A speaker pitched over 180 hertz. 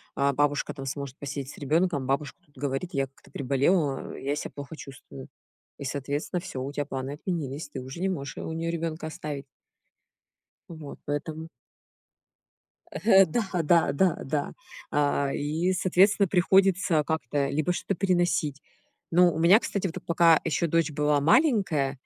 No: medium, 150 Hz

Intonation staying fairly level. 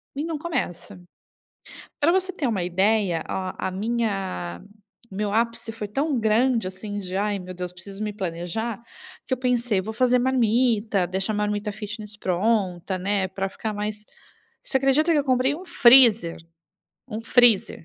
No: average, 4.2 semitones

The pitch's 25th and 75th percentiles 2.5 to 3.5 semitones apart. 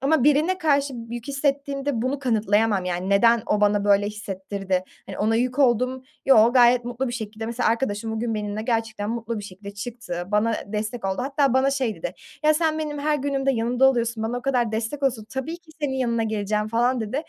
No: average, 4.1 semitones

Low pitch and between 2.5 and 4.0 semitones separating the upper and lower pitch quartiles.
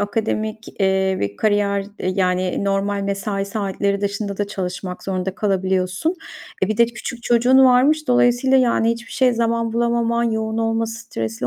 No: high, 215 Hz; average, 3.3 semitones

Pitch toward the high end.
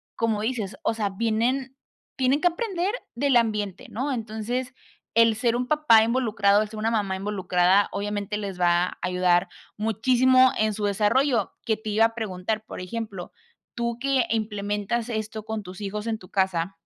Yes: high, 220 Hz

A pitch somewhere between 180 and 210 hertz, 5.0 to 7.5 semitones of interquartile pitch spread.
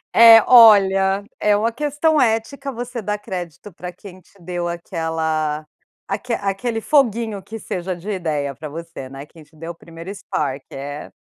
Yes: high, 190 Hz; wide, 5.5 semitones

